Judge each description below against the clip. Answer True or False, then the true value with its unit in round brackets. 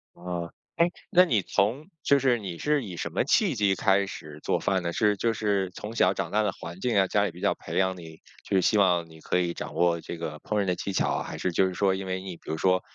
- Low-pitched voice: True (95 Hz)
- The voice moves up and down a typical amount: True (3.4 semitones)